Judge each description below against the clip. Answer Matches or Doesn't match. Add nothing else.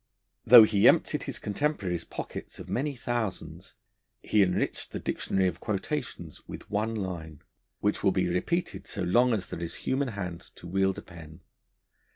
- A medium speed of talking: Matches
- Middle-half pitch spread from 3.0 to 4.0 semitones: Doesn't match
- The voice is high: Doesn't match